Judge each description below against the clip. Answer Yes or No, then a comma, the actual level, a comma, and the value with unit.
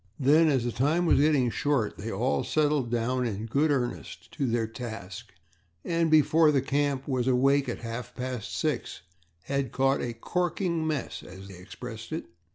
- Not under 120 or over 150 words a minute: No, average, 170 wpm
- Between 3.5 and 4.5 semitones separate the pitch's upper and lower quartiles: Yes, average, 4.1 semitones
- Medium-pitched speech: No, low, 130 Hz